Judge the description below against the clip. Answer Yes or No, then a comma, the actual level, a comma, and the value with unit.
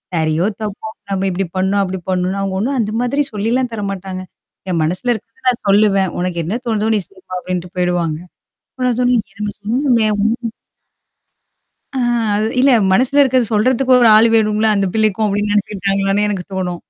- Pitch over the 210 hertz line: No, high, 205 Hz